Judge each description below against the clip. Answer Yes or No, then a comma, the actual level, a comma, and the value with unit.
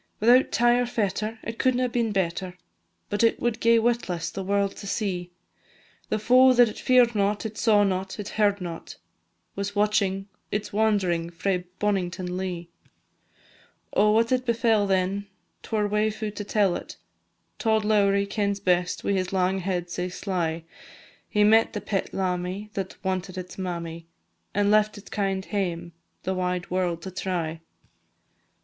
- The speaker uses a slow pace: No, average, 160 wpm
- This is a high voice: Yes, high, 200 Hz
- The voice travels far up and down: No, average, 2.8 semitones